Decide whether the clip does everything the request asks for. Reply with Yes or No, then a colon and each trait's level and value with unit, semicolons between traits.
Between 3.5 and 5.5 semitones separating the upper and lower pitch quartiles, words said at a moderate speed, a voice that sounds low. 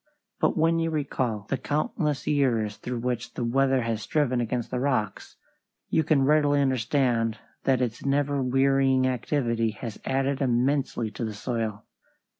No: average, 3.1 semitones; average, 150 wpm; low, 130 Hz